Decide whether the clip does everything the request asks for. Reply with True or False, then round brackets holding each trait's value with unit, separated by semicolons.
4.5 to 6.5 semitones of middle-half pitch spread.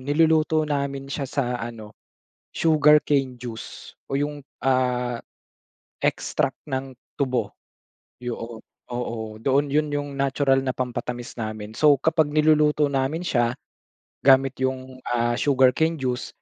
False (3.0 semitones)